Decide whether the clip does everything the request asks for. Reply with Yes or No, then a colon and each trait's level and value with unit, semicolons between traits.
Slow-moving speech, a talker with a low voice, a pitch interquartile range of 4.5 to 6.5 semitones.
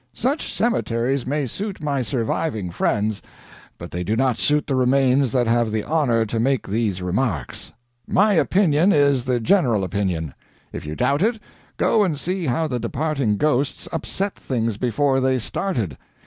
No: average, 160 wpm; low, 130 Hz; average, 5.2 semitones